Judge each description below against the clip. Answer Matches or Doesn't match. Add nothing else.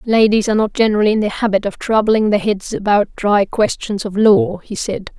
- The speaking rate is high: Matches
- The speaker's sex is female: Matches